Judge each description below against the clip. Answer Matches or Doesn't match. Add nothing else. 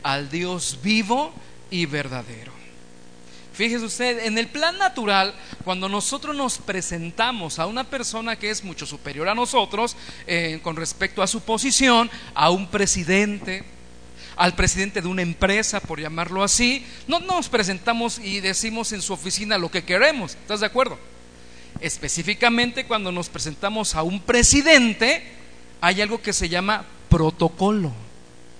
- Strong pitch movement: Matches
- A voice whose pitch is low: Doesn't match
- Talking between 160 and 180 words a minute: Doesn't match